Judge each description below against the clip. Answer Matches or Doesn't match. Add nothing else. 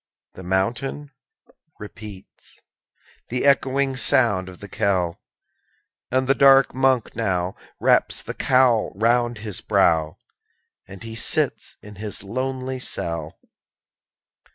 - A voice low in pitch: Matches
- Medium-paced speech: Doesn't match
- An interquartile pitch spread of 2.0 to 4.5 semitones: Doesn't match